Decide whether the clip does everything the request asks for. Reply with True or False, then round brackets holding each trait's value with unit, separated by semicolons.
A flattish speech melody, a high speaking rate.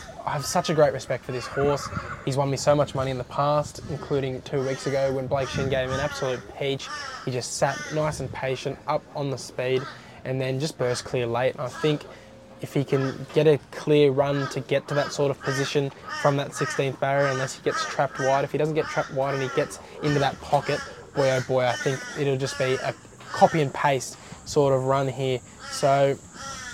True (1.6 semitones; 225 wpm)